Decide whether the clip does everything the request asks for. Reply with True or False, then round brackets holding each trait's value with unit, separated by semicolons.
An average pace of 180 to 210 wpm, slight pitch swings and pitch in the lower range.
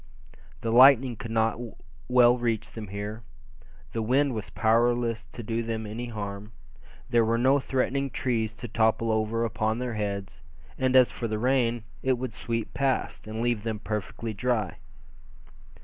False (160 wpm; 2.0 semitones; 115 Hz)